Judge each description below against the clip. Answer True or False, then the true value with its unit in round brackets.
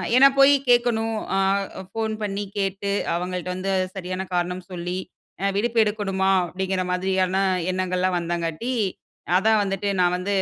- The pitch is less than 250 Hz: True (190 Hz)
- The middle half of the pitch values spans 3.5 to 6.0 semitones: False (2.4 semitones)